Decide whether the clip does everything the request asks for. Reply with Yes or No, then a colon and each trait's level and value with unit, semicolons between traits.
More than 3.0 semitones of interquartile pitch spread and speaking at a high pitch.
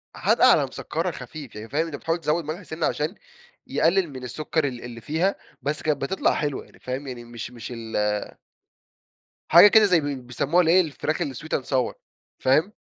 No: average, 4.5 semitones; medium, 145 Hz